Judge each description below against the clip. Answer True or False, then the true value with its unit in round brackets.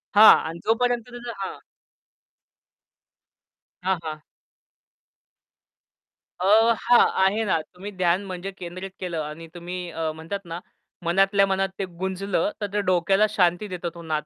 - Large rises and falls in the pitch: False (3.0 semitones)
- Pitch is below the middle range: False (185 Hz)